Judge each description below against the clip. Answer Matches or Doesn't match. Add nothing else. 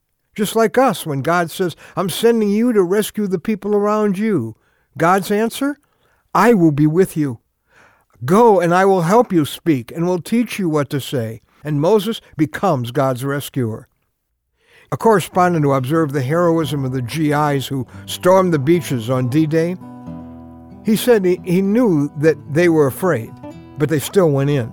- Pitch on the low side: Doesn't match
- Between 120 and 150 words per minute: Doesn't match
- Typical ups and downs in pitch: Doesn't match